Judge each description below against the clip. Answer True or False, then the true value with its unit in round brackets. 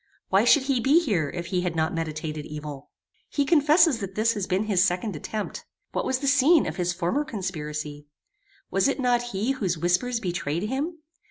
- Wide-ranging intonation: True (7.7 semitones)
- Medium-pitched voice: False (195 Hz)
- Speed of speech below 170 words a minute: False (190 wpm)